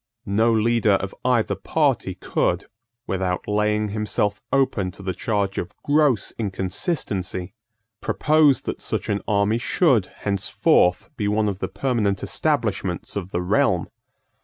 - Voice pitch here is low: Yes, low, 105 Hz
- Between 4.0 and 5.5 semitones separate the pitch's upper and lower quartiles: No, average, 3.2 semitones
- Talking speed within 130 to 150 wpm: Yes, slow, 135 wpm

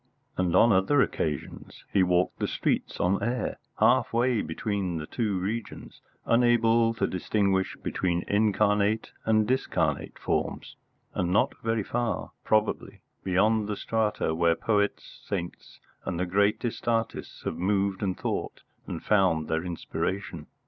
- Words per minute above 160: No, slow, 135 wpm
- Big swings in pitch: No, average, 3.5 semitones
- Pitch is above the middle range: No, low, 100 Hz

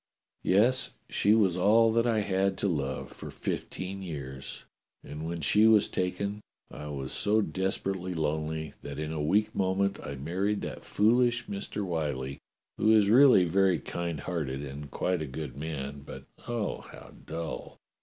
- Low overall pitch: Yes, very low, 90 Hz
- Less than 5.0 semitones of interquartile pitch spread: No, wide, 5.4 semitones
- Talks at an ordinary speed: Yes, average, 160 wpm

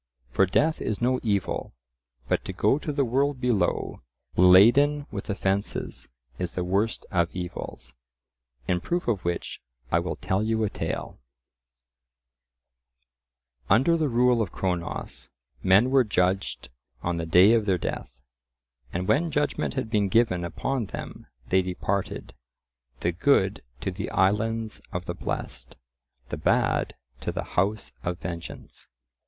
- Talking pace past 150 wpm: No, average, 140 wpm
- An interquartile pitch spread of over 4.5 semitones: Yes, average, 5.2 semitones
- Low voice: Yes, low, 100 Hz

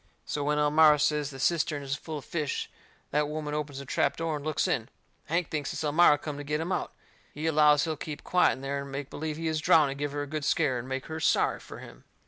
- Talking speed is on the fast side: Yes, fast, 260 wpm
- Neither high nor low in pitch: Yes, medium, 150 Hz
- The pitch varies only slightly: Yes, narrow, 1.7 semitones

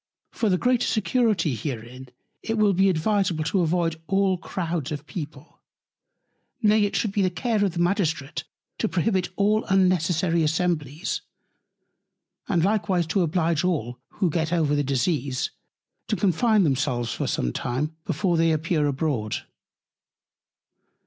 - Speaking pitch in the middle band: Yes, medium, 170 Hz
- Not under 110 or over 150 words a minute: Yes, average, 140 wpm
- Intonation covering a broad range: No, average, 4.4 semitones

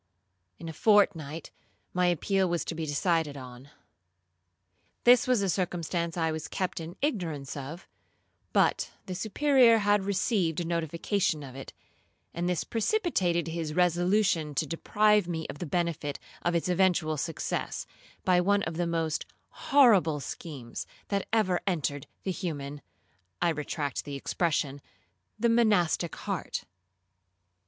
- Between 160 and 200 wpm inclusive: No, slow, 135 wpm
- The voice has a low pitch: No, medium, 170 Hz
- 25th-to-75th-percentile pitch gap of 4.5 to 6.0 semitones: No, average, 3.8 semitones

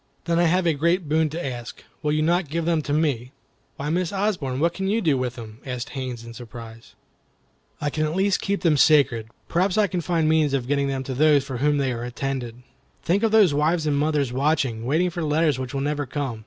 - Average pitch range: Yes, average, 4.4 semitones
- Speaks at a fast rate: Yes, fast, 235 wpm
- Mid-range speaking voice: Yes, medium, 150 Hz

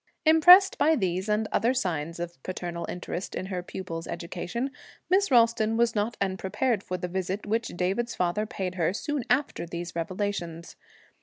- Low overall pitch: No, high, 190 Hz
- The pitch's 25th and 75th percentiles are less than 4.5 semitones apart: No, average, 5.0 semitones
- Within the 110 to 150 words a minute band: No, average, 160 wpm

